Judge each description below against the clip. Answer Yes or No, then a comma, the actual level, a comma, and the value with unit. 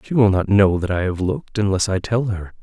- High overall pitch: No, low, 100 Hz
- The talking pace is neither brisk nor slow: No, fast, 275 wpm